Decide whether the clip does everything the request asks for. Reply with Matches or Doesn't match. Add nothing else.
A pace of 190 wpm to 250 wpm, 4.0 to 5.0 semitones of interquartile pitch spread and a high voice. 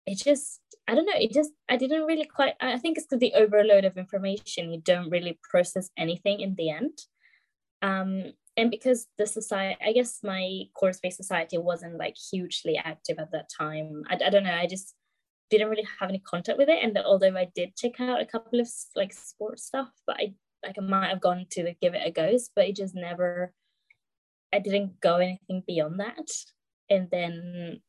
Matches